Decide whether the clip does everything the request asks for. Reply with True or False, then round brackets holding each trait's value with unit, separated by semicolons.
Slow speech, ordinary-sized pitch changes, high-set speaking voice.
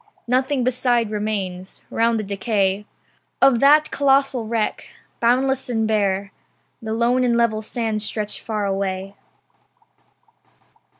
True (115 wpm; 3.3 semitones; 225 Hz)